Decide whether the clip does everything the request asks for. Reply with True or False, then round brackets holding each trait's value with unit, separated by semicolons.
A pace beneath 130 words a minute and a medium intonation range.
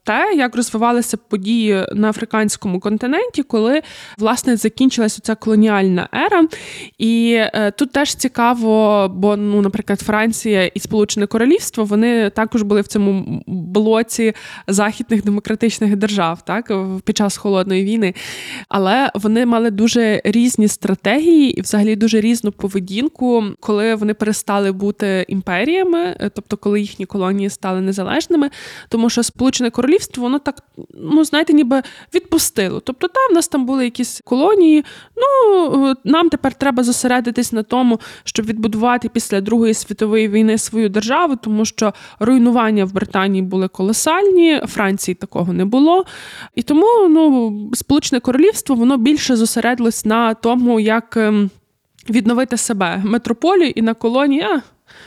False (135 wpm; 3.9 semitones)